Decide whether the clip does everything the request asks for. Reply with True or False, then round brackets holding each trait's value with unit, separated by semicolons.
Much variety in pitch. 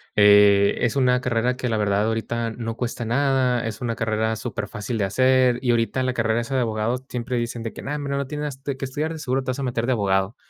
False (2.6 semitones)